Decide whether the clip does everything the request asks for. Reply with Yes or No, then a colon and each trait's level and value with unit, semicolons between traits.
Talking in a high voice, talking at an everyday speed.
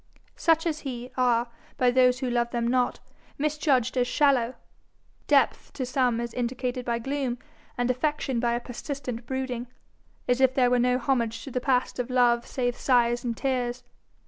Yes: very high, 250 Hz; average, 170 wpm